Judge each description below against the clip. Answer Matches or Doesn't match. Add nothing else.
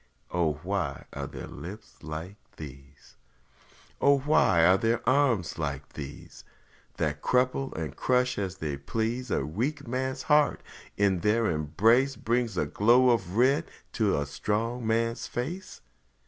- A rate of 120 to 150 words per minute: Matches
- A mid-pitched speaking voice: Doesn't match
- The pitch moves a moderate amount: Doesn't match